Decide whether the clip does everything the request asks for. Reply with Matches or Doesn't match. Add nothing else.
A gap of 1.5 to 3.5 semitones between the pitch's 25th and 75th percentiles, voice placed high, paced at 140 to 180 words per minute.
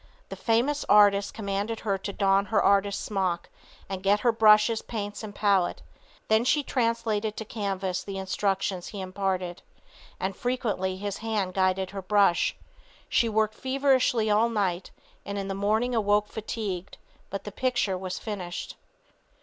Matches